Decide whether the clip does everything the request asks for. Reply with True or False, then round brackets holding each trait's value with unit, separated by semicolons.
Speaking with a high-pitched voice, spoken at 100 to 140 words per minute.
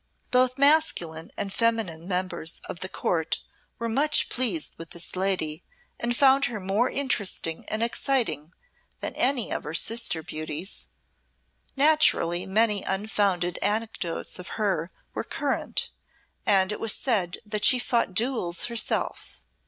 True (205 Hz; 135 wpm)